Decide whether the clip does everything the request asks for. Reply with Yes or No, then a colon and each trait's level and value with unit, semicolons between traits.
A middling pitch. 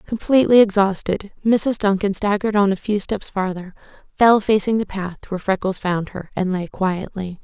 No: high, 200 Hz